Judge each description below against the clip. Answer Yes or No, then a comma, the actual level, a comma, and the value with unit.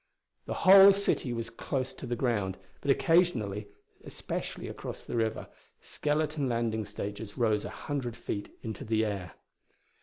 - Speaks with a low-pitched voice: Yes, low, 115 Hz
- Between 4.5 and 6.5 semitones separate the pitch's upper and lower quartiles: Yes, average, 4.8 semitones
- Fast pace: No, average, 145 wpm